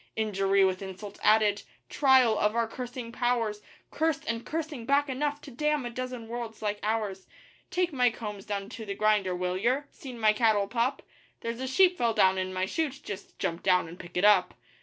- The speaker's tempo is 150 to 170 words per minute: No, average, 200 wpm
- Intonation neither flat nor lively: Yes, average, 4.2 semitones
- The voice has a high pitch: Yes, high, 225 Hz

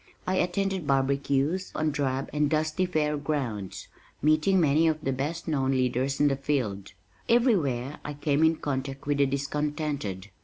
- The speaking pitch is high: No, medium, 145 Hz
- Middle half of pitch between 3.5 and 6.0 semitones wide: No, narrow, 2.6 semitones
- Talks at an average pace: Yes, average, 155 wpm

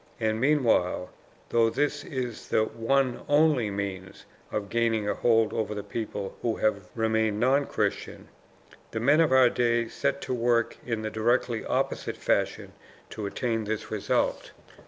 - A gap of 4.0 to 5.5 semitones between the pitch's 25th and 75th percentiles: No, narrow, 2.6 semitones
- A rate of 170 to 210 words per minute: No, average, 155 wpm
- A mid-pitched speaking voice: No, low, 115 Hz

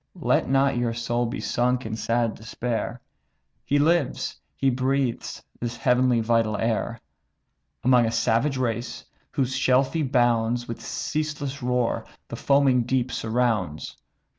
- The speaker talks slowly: Yes, slow, 130 wpm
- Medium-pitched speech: No, low, 125 Hz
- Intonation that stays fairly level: Yes, narrow, 2.2 semitones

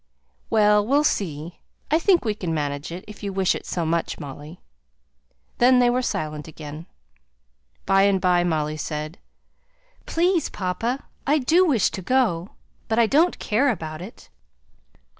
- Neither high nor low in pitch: No, high, 195 Hz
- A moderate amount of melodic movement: No, wide, 7.5 semitones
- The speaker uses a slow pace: No, average, 160 wpm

